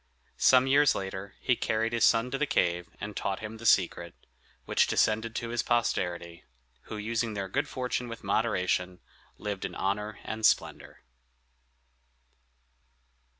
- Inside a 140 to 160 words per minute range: Yes, average, 145 wpm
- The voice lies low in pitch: Yes, low, 110 Hz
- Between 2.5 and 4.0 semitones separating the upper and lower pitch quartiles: Yes, average, 3.4 semitones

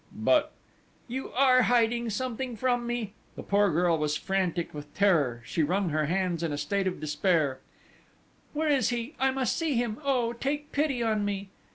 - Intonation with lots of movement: Yes, wide, 6.5 semitones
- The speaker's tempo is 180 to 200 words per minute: Yes, average, 185 wpm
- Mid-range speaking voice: No, high, 215 Hz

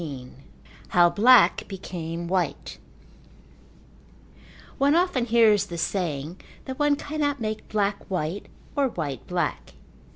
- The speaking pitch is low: No, high, 200 Hz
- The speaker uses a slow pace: Yes, slow, 110 wpm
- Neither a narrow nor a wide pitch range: No, wide, 6.9 semitones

